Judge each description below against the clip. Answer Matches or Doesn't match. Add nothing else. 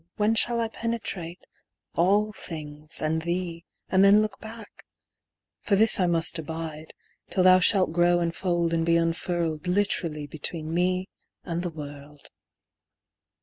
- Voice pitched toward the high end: Doesn't match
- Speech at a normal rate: Matches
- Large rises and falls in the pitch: Doesn't match